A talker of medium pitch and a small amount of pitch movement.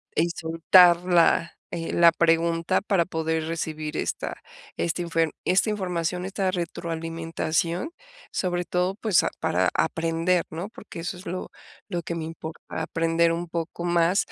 Yes: medium, 170 Hz; narrow, 1.5 semitones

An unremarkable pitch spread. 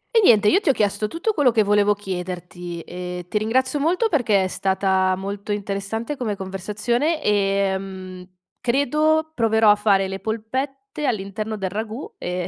Yes: average, 4.4 semitones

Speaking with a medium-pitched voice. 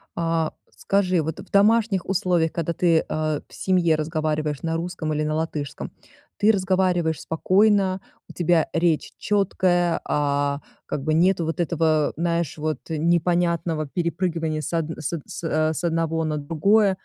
Yes: medium, 165 Hz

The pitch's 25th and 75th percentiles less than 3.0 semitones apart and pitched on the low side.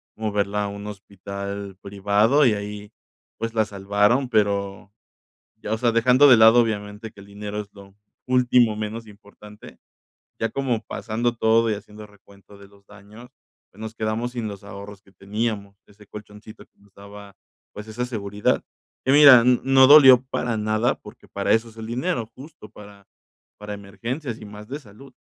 Yes: narrow, 2.5 semitones; low, 105 Hz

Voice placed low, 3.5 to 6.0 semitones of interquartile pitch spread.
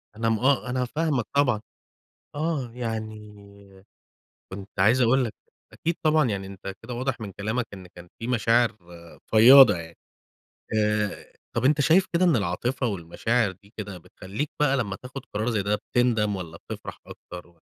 Yes: low, 110 Hz; average, 4.1 semitones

